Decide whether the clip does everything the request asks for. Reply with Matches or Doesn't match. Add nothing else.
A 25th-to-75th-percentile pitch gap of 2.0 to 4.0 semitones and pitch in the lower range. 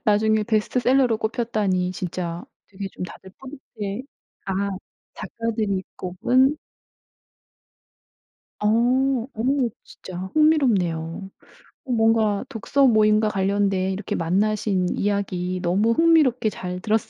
Doesn't match